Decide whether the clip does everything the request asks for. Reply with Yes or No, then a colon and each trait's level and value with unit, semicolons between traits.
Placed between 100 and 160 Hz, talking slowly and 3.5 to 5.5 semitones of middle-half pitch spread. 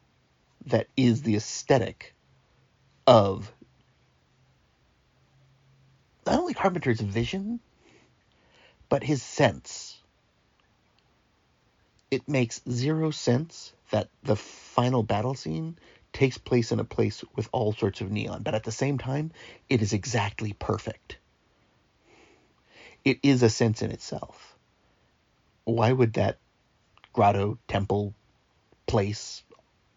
Yes: low, 120 Hz; slow, 105 wpm; average, 4.0 semitones